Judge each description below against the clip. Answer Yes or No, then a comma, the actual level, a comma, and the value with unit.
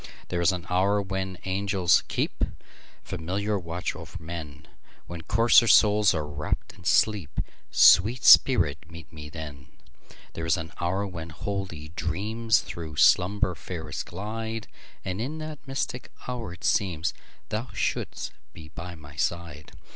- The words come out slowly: Yes, slow, 120 wpm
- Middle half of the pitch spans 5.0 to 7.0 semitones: No, average, 4.2 semitones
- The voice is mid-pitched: No, very low, 90 Hz